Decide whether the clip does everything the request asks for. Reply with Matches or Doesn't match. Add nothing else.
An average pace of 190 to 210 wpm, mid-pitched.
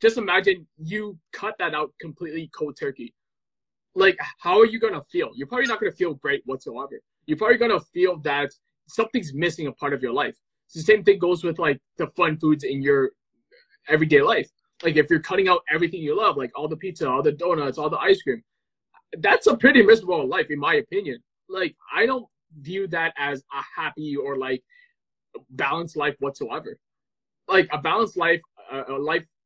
Matches